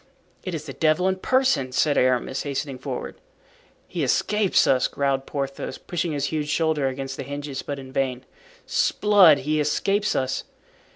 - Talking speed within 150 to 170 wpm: Yes, average, 160 wpm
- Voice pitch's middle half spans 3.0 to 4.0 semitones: Yes, average, 3.4 semitones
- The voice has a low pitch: No, medium, 145 Hz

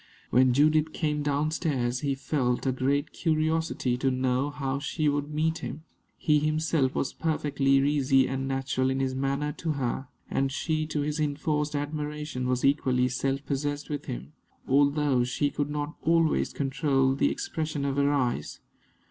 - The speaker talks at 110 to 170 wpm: Yes, average, 165 wpm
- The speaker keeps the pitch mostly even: Yes, narrow, 2.1 semitones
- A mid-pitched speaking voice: Yes, medium, 145 Hz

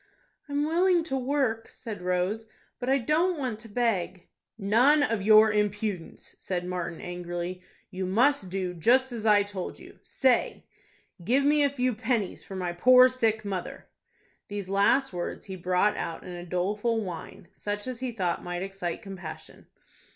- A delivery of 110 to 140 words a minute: No, average, 165 wpm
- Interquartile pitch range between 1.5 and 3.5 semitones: No, wide, 5.6 semitones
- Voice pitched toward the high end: Yes, high, 210 Hz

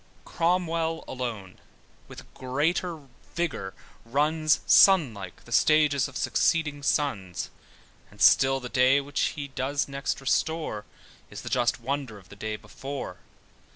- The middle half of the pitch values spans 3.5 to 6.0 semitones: Yes, average, 4.3 semitones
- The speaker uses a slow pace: Yes, slow, 130 wpm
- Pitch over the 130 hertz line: Yes, medium, 140 Hz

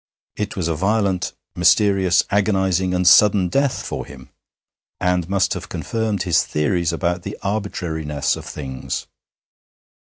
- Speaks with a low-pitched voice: Yes, very low, 90 Hz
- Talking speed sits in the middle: No, slow, 130 wpm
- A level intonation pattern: No, average, 3.2 semitones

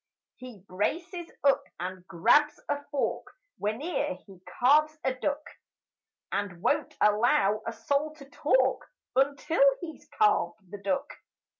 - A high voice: Yes, very high, 265 Hz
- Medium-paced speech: No, slow, 125 wpm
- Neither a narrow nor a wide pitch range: No, wide, 6.4 semitones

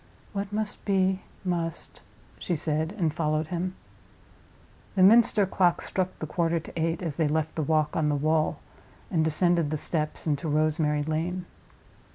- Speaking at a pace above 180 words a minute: No, average, 160 wpm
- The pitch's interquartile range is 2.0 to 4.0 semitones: Yes, average, 2.8 semitones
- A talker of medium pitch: Yes, medium, 165 Hz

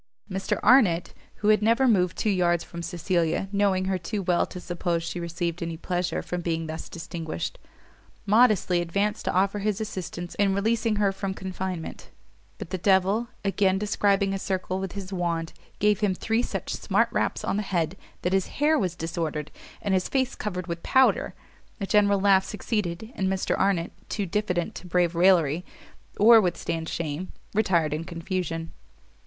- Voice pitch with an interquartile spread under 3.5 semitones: Yes, average, 3.0 semitones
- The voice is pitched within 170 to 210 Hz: Yes, medium, 185 Hz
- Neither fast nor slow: Yes, average, 170 wpm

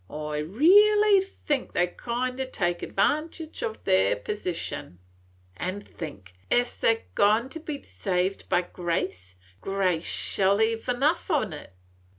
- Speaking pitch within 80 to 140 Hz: No, high, 205 Hz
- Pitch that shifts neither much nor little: No, wide, 7.7 semitones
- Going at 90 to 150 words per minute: Yes, average, 140 wpm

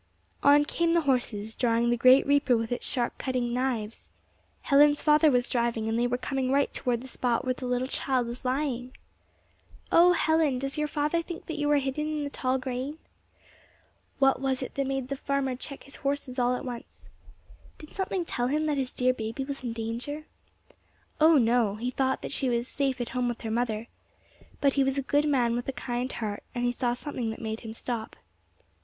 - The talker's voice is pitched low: No, very high, 255 Hz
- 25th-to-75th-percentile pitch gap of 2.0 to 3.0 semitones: Yes, average, 2.7 semitones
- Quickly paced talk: Yes, fast, 210 wpm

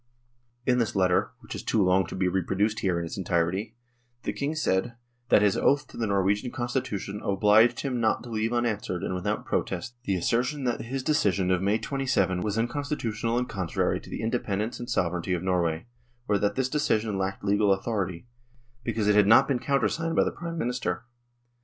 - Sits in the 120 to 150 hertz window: No, low, 105 Hz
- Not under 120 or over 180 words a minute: No, average, 195 wpm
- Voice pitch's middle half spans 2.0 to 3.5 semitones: No, average, 4.3 semitones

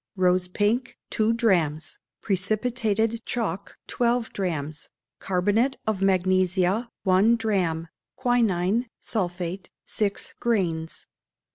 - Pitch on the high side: Yes, high, 195 Hz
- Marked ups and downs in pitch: No, average, 4.0 semitones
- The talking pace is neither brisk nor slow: No, slow, 90 wpm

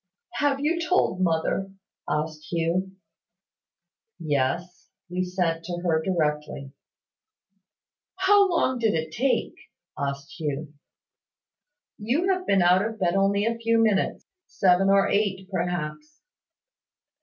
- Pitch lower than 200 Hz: Yes, medium, 185 Hz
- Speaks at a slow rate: Yes, slow, 115 wpm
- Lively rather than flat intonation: Yes, wide, 5.8 semitones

